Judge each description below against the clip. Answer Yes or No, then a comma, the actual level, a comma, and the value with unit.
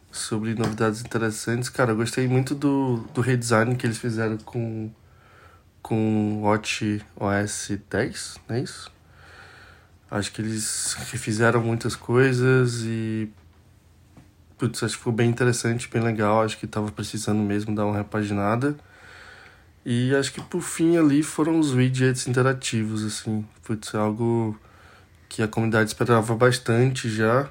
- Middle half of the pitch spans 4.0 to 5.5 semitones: No, average, 2.7 semitones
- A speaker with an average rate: Yes, average, 140 wpm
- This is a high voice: No, low, 110 Hz